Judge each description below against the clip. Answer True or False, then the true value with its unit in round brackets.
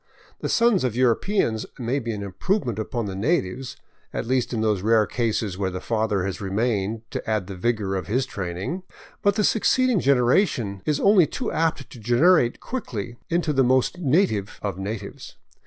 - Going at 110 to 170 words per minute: False (180 wpm)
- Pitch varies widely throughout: True (6.6 semitones)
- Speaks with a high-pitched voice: False (120 Hz)